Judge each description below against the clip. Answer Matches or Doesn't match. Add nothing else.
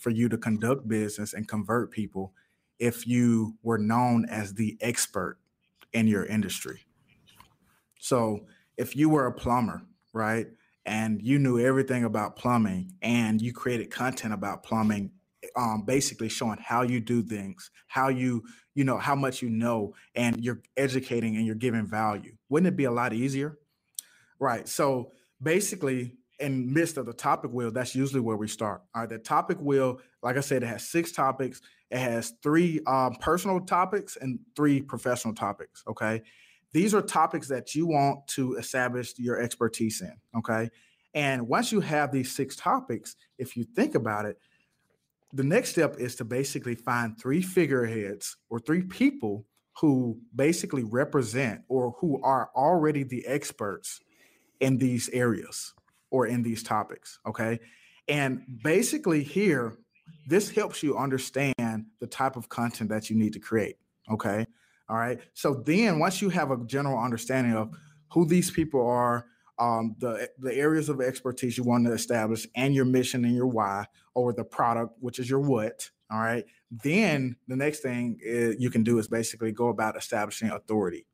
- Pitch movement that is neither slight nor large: Matches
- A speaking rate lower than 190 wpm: Matches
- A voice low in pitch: Matches